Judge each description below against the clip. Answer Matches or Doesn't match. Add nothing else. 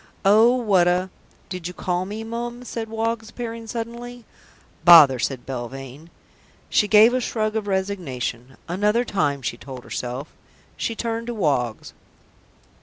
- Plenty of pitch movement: Matches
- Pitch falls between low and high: Doesn't match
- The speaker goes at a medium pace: Matches